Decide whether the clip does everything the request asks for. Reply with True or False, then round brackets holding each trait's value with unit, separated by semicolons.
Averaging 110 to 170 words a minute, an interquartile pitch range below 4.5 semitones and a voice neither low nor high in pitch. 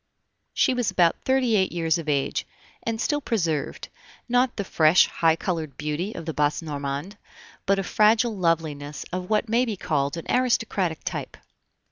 False (165 wpm; 6.2 semitones; 175 Hz)